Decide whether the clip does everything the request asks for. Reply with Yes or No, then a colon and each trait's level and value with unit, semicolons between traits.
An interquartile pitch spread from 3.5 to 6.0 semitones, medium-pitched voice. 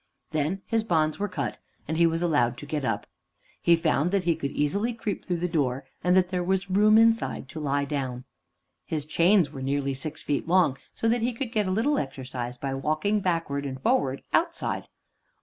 Yes: wide, 5.5 semitones; medium, 165 Hz